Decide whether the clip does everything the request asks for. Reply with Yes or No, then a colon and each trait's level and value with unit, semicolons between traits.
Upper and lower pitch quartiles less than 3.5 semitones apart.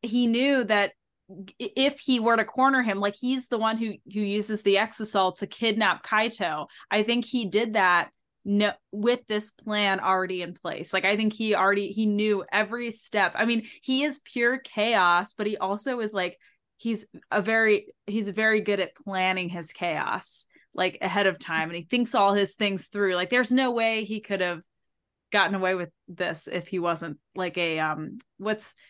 Yes: average, 3.1 semitones